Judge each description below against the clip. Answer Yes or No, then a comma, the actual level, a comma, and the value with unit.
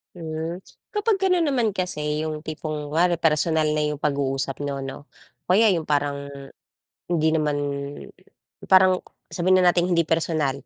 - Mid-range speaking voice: Yes, medium, 160 Hz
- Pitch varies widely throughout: No, average, 3.1 semitones